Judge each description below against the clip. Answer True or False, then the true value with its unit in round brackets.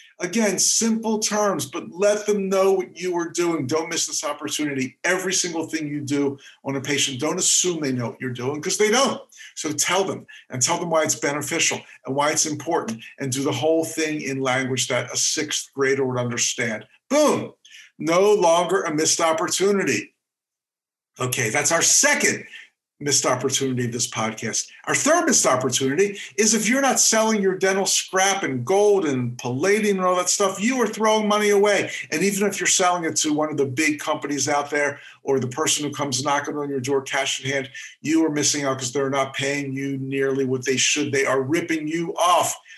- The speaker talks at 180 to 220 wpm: True (200 wpm)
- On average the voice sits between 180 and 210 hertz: False (155 Hz)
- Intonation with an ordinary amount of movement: False (5.8 semitones)